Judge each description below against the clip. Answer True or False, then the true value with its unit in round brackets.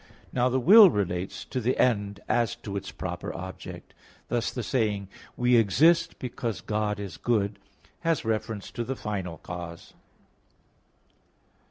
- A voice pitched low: True (110 Hz)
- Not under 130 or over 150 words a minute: True (140 wpm)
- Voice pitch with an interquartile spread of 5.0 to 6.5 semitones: False (3.8 semitones)